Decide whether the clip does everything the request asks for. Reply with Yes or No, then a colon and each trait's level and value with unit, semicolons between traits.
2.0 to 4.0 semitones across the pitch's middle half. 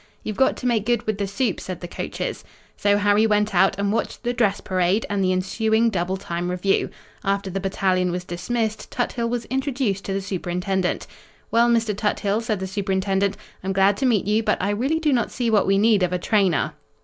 Yes: average, 3.0 semitones